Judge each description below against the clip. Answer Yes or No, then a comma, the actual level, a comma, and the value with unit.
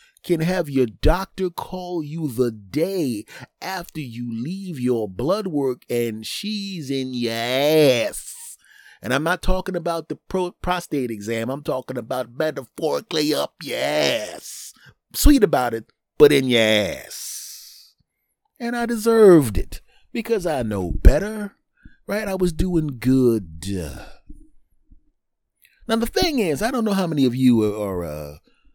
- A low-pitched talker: No, medium, 150 Hz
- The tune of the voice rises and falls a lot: Yes, wide, 7.7 semitones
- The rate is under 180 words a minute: Yes, average, 145 wpm